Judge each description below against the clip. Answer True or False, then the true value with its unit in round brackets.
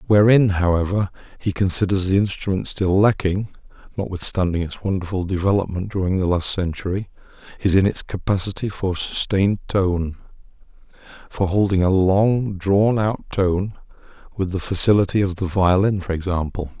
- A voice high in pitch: False (95 Hz)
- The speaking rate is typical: False (130 wpm)